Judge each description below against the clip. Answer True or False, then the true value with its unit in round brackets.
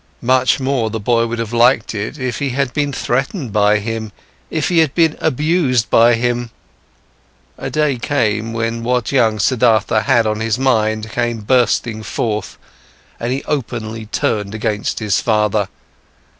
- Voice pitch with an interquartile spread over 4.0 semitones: False (3.0 semitones)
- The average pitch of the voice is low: True (115 Hz)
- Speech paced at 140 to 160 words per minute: True (155 wpm)